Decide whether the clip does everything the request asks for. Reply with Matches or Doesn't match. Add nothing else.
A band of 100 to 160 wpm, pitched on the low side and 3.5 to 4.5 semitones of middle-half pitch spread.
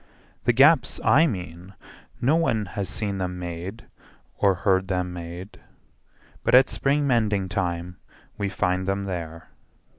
Matches